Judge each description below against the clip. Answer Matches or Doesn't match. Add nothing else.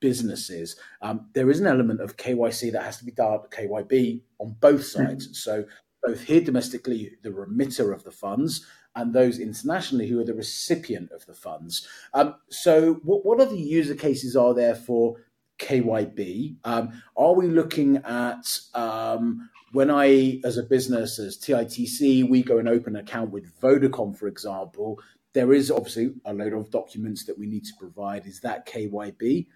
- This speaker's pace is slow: Doesn't match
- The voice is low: Matches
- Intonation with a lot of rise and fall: Doesn't match